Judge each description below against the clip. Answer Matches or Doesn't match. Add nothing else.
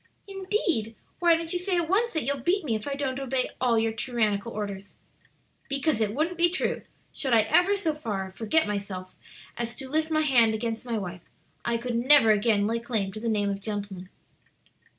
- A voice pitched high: Matches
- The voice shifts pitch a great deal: Matches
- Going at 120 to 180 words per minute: Doesn't match